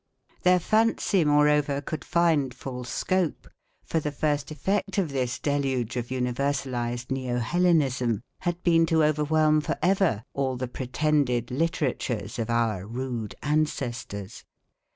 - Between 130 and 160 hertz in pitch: Yes, medium, 140 Hz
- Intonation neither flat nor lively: Yes, average, 4.2 semitones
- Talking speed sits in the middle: No, slow, 130 wpm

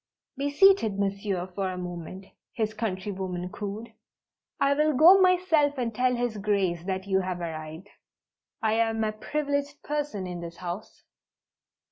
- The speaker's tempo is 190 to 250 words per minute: No, average, 145 wpm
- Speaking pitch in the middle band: No, high, 210 Hz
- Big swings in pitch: Yes, wide, 7.1 semitones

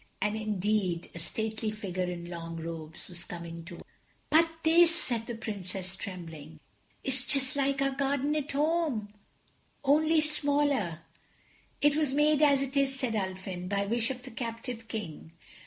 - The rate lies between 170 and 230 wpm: No, average, 155 wpm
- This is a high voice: Yes, high, 225 Hz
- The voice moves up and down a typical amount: No, wide, 7.4 semitones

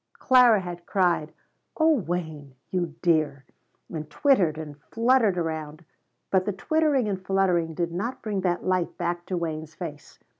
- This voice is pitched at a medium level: Yes, medium, 175 Hz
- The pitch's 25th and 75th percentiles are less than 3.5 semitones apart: No, average, 3.9 semitones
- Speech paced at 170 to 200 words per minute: No, average, 150 wpm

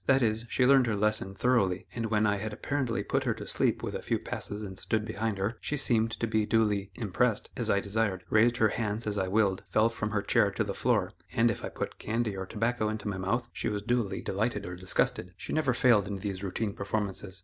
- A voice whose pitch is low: Yes, low, 110 Hz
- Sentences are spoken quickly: Yes, fast, 235 wpm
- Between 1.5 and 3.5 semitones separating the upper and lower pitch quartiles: Yes, narrow, 2.5 semitones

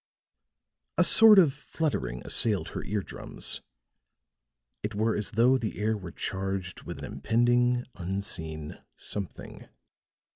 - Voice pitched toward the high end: No, low, 105 Hz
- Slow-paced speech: Yes, slow, 120 wpm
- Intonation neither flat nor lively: Yes, average, 4.4 semitones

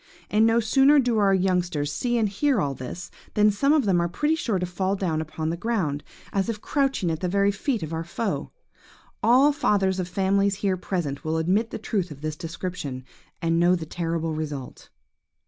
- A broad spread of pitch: No, average, 4.8 semitones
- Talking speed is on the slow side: No, average, 200 wpm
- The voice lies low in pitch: No, medium, 185 Hz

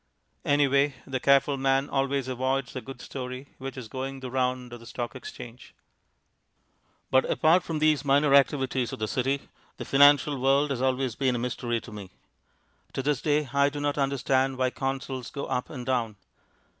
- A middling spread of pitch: No, narrow, 1.7 semitones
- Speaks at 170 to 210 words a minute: Yes, average, 180 wpm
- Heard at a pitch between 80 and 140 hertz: Yes, low, 135 Hz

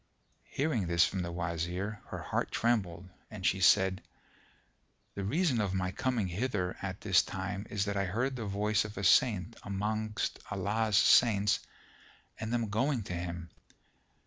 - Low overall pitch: Yes, low, 100 Hz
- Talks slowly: No, average, 155 wpm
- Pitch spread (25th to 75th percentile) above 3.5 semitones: No, average, 3.1 semitones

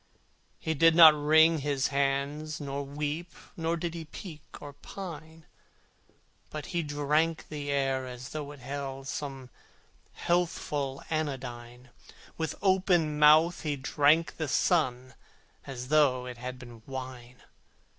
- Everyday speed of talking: No, slow, 130 wpm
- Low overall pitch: No, medium, 145 Hz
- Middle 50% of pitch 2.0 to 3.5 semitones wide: Yes, average, 3.1 semitones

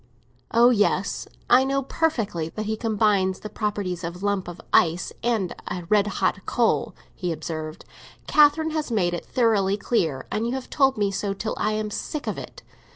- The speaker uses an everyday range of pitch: Yes, average, 4.4 semitones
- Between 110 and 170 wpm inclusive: No, average, 185 wpm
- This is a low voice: No, high, 210 Hz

